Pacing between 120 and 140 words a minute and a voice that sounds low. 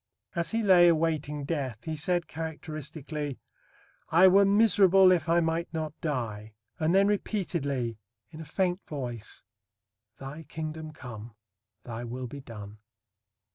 No: slow, 135 wpm; medium, 155 Hz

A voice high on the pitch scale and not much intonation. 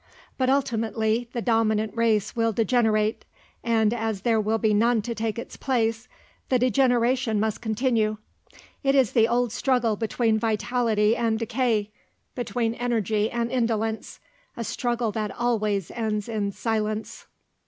Yes: high, 225 Hz; narrow, 1.8 semitones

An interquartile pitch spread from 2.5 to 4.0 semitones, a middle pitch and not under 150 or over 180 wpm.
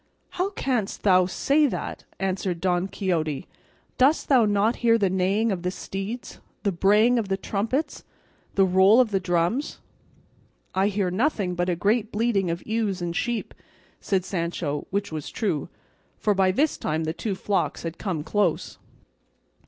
No: average, 3.7 semitones; high, 195 Hz; average, 160 wpm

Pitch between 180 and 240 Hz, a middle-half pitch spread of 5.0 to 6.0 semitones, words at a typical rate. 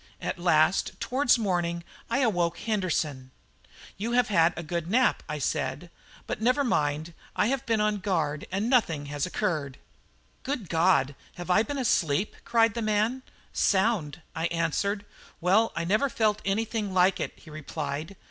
Yes: high, 190 Hz; wide, 5.4 semitones; average, 155 wpm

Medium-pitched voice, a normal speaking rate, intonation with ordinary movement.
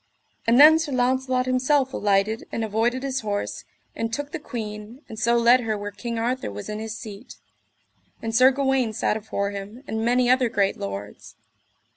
No: high, 230 Hz; average, 180 wpm; average, 3.3 semitones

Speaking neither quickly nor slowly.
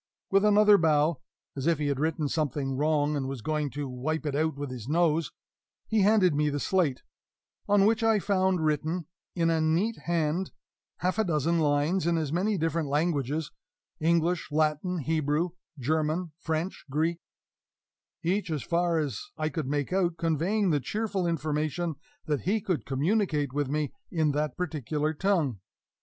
Yes: average, 165 wpm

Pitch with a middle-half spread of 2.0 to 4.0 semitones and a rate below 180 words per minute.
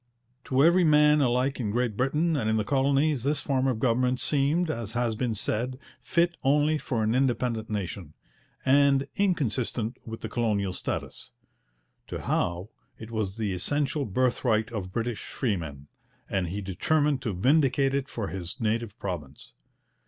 No: average, 4.6 semitones; average, 155 wpm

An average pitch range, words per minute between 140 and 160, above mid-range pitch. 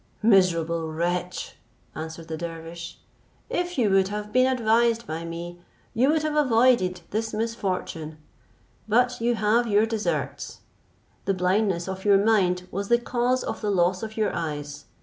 Yes: average, 5.0 semitones; average, 150 wpm; high, 200 Hz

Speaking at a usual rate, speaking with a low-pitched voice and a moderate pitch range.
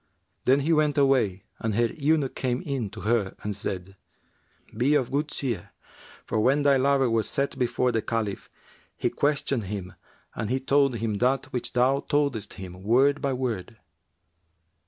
Yes: average, 165 wpm; low, 125 Hz; average, 4.2 semitones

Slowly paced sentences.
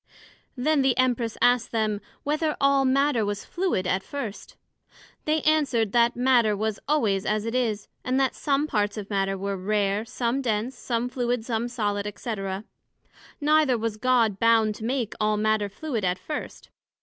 No: average, 165 wpm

